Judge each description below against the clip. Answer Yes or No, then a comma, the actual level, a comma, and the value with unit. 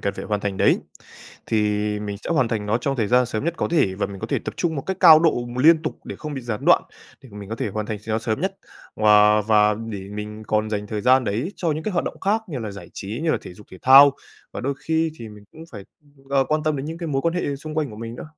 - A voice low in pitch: Yes, low, 120 Hz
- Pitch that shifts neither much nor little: No, wide, 6.5 semitones